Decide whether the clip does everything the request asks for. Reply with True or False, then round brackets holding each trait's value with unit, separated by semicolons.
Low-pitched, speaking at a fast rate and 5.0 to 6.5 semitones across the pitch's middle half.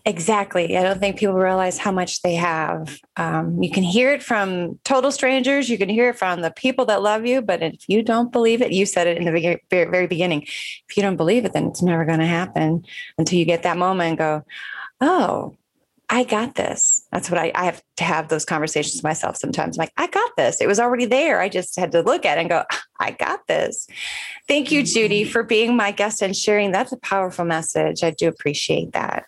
False (185 Hz; 230 wpm; 5.3 semitones)